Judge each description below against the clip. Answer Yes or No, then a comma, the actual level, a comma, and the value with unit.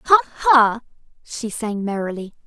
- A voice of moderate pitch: No, high, 215 Hz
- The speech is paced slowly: Yes, slow, 120 wpm